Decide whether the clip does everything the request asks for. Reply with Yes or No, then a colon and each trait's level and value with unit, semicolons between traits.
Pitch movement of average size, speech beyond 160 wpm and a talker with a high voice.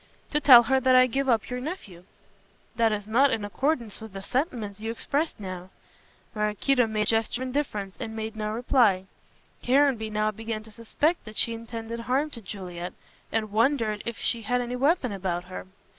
Yes: average, 3.2 semitones; average, 190 wpm; high, 225 Hz